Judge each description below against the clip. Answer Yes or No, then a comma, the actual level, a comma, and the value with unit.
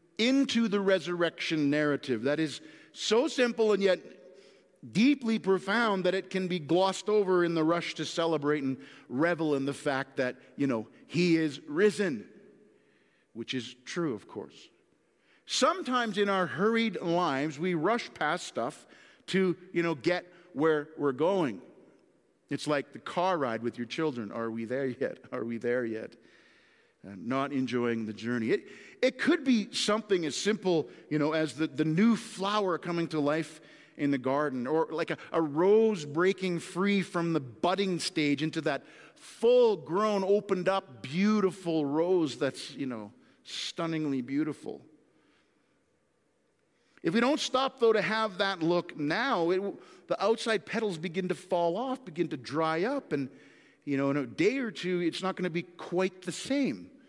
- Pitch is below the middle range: No, medium, 175 Hz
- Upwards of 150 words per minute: Yes, average, 165 wpm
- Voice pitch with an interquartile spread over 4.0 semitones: Yes, average, 5.1 semitones